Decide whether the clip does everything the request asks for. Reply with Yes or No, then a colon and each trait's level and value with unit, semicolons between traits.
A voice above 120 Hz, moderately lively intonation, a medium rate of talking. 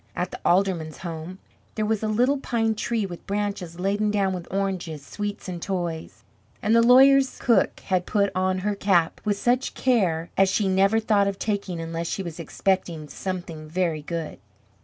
Yes: high, 190 Hz; average, 3.5 semitones; average, 180 wpm